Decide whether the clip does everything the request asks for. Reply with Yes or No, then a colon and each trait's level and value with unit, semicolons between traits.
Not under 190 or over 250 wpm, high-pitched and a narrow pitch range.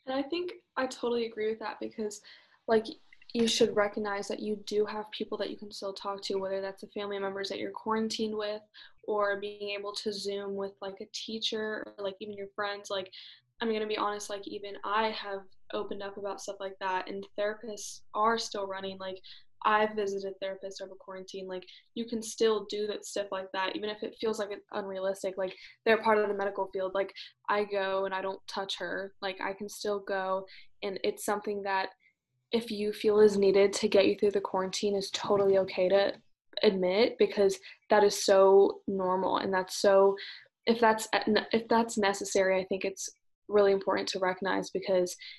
Yes: average, 200 wpm; high, 205 Hz; narrow, 1.7 semitones